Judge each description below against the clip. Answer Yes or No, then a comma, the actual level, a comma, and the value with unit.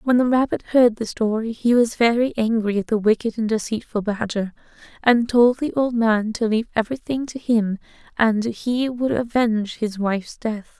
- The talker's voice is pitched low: No, high, 225 Hz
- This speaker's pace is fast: No, average, 185 wpm